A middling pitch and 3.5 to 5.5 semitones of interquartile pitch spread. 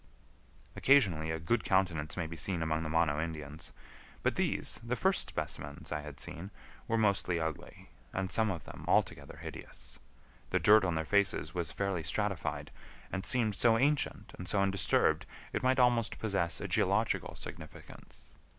No: very low, 90 Hz; average, 5.1 semitones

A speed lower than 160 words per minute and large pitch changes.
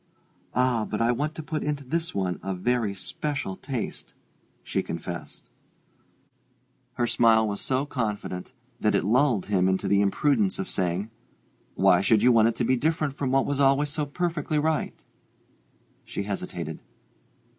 No: average, 165 wpm; wide, 6.0 semitones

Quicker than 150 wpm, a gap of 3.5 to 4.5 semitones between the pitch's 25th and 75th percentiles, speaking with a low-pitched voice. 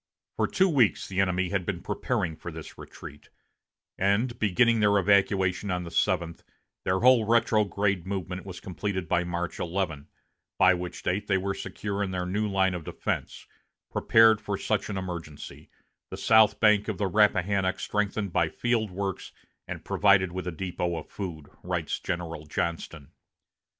No: average, 160 wpm; average, 2.8 semitones; very low, 95 Hz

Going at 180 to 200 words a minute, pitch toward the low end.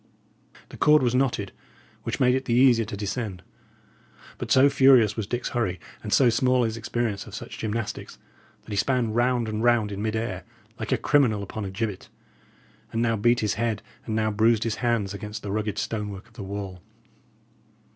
Yes: average, 190 wpm; low, 110 Hz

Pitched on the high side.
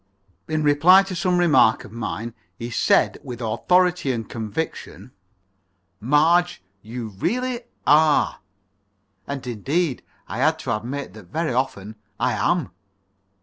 No: medium, 140 Hz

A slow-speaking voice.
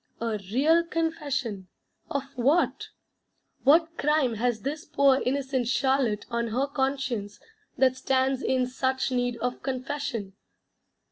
Yes: slow, 120 wpm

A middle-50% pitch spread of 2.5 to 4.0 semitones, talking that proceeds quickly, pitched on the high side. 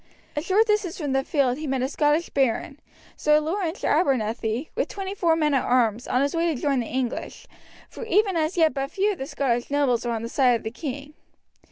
No: average, 4.8 semitones; fast, 225 wpm; very high, 285 Hz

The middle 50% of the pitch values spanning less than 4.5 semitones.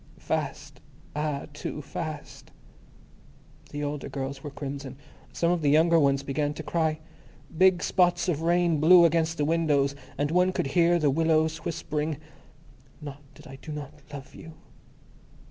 Yes: average, 2.8 semitones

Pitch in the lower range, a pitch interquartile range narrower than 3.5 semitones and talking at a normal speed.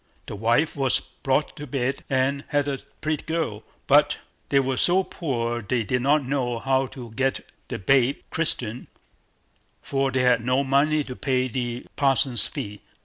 Yes: low, 130 Hz; narrow, 2.4 semitones; average, 165 wpm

